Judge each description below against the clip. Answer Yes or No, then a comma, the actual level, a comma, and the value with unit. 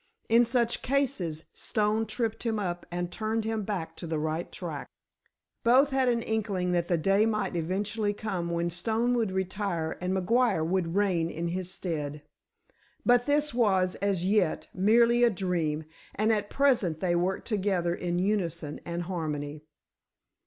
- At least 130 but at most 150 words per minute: No, average, 160 wpm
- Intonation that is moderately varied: Yes, average, 4.5 semitones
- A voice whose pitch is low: No, high, 190 Hz